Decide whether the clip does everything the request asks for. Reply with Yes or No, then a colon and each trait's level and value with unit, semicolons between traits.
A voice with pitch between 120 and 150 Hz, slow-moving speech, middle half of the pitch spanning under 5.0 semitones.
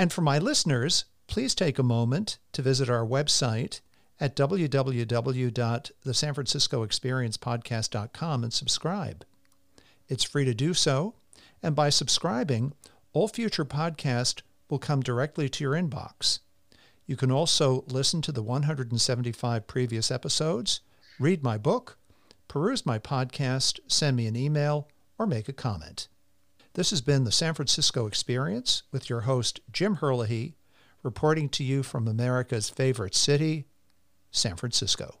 Yes: low, 135 Hz; slow, 130 wpm; average, 3.9 semitones